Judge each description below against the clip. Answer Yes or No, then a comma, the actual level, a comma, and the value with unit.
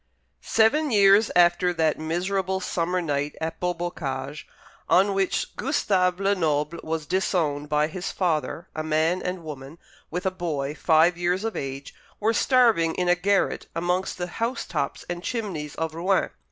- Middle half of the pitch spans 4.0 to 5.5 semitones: No, average, 3.3 semitones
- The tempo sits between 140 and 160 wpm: Yes, average, 150 wpm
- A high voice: No, medium, 175 Hz